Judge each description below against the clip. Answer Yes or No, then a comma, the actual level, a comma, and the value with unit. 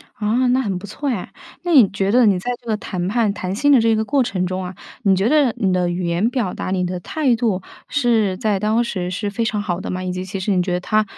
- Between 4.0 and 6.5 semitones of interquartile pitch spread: Yes, average, 4.3 semitones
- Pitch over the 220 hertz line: No, high, 205 Hz